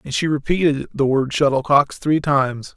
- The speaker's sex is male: Yes, male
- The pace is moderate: Yes, average, 175 wpm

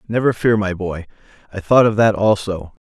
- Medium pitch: No, low, 105 Hz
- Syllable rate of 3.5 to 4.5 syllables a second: No, 5.1 syllables/s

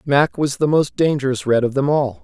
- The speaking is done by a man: Yes, male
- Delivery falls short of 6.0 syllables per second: Yes, 5.2 syllables/s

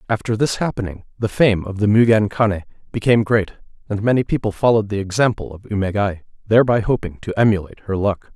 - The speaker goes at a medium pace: Yes, average, 170 wpm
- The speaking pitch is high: No, low, 105 Hz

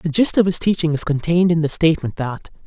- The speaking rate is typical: No, fast, 250 wpm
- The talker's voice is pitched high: No, medium, 165 Hz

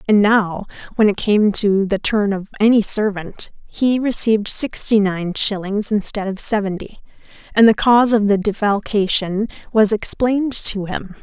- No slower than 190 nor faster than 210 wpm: No, average, 155 wpm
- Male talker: No, female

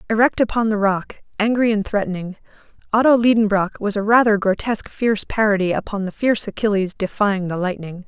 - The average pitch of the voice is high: Yes, high, 210 Hz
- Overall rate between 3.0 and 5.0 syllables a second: No, 5.9 syllables/s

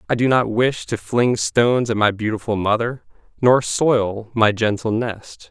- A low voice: Yes, low, 115 Hz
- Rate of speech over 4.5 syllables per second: No, 4.3 syllables/s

